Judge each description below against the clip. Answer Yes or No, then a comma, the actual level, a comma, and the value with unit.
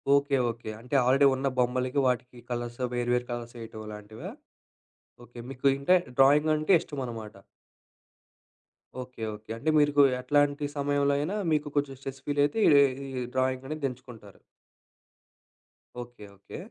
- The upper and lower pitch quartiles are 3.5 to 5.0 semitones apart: No, average, 2.9 semitones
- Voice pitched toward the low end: Yes, low, 130 Hz